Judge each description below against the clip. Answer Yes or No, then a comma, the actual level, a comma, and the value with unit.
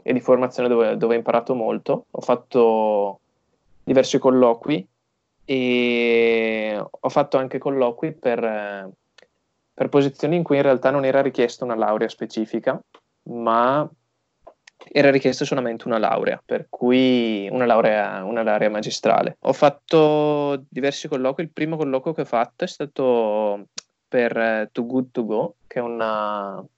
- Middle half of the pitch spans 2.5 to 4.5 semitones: Yes, average, 3.3 semitones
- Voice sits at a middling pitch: No, low, 125 Hz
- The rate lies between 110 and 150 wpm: Yes, average, 140 wpm